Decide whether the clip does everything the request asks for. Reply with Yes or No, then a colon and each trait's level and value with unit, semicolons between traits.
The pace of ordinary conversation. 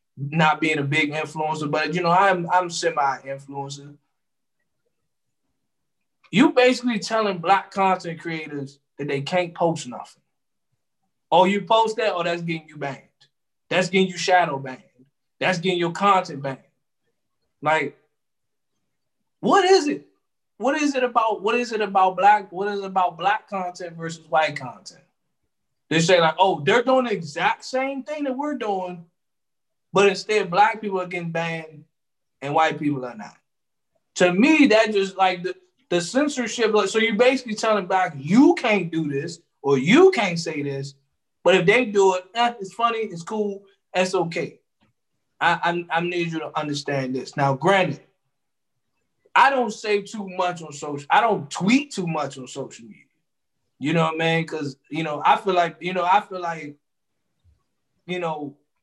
Yes: average, 170 wpm